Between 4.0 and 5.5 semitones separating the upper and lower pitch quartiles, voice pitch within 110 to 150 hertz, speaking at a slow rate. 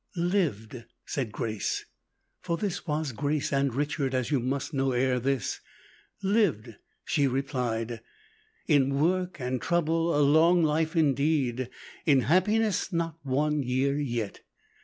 Yes: average, 4.3 semitones; medium, 140 Hz; slow, 130 wpm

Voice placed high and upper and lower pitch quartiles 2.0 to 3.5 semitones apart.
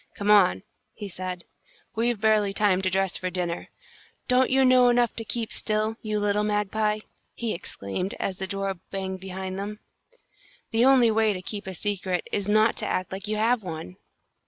Yes: high, 205 Hz; narrow, 2.6 semitones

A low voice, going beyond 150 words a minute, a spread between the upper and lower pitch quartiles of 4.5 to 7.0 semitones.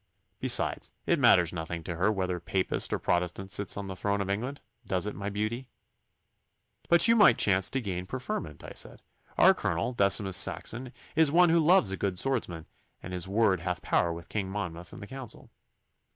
Yes: low, 100 Hz; average, 190 wpm; average, 4.9 semitones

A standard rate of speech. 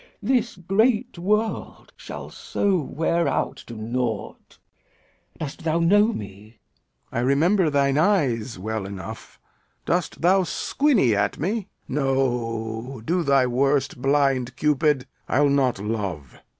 No: slow, 125 wpm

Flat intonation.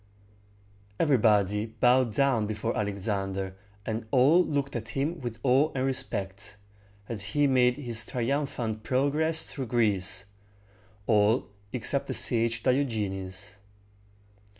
No: average, 4.4 semitones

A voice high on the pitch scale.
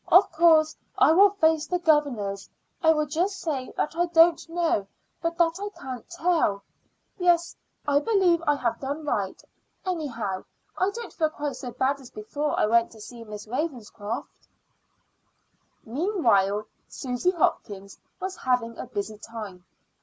Yes: very high, 290 Hz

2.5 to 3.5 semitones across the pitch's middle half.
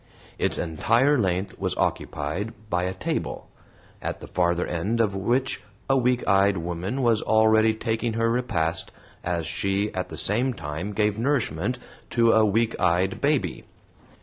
No: average, 4.6 semitones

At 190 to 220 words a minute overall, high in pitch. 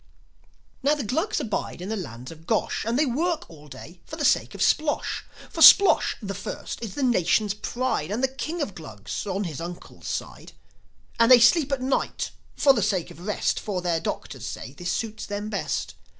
Yes: average, 200 wpm; high, 210 Hz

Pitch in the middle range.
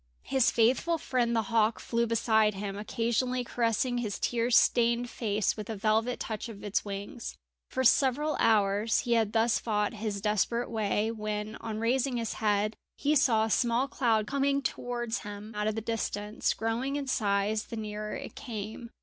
No: high, 225 Hz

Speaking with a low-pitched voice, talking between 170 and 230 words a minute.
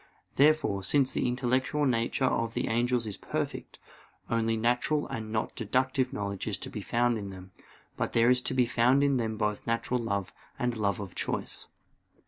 Yes: low, 120 Hz; average, 180 wpm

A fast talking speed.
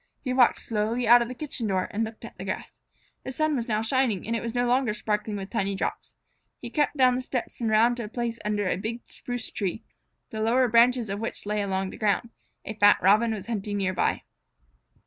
Yes: fast, 230 wpm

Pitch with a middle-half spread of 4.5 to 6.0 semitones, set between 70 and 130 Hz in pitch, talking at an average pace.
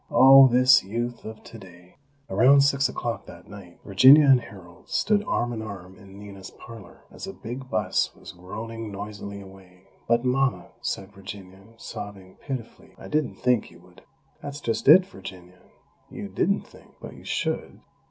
Yes: average, 4.9 semitones; low, 110 Hz; average, 165 wpm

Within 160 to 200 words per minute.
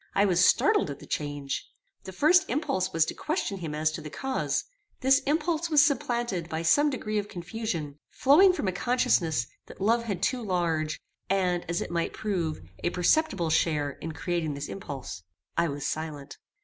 Yes: average, 180 wpm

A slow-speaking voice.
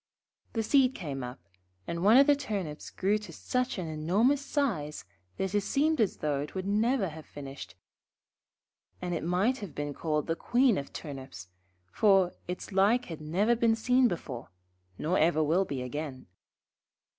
No: average, 170 wpm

